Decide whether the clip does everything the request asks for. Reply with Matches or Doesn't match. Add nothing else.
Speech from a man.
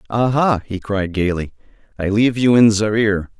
Matches